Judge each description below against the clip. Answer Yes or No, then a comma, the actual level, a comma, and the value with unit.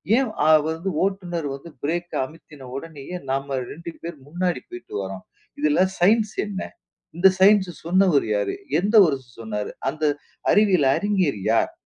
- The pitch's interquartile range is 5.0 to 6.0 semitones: Yes, wide, 5.6 semitones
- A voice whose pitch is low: No, medium, 170 Hz